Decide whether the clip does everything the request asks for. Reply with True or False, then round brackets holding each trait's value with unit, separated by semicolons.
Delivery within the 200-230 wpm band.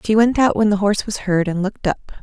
False (295 wpm)